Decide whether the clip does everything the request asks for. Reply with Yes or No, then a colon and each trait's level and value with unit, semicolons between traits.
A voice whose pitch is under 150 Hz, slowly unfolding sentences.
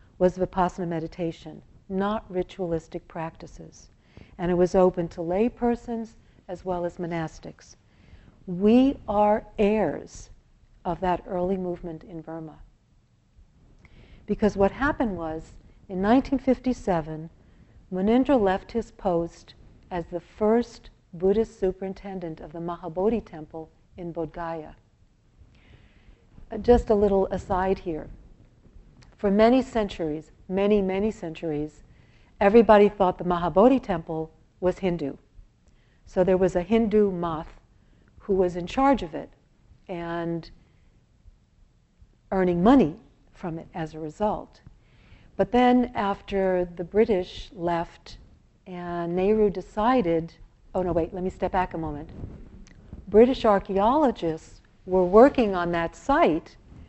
No: medium, 185 Hz; slow, 115 wpm